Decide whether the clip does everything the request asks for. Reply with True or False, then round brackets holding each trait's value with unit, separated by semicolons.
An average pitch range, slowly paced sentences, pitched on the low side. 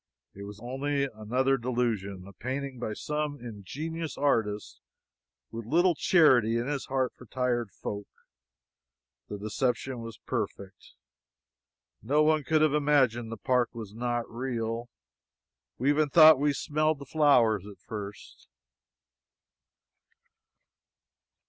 True (4.5 semitones; 120 wpm; 125 Hz)